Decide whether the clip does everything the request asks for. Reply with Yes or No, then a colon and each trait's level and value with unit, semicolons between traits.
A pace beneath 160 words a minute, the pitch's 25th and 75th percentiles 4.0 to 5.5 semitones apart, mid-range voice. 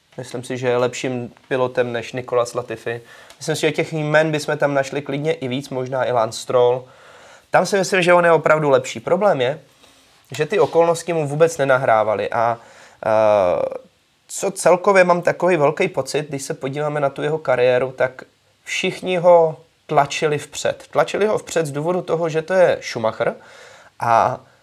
No: fast, 170 wpm; average, 4.7 semitones; medium, 145 Hz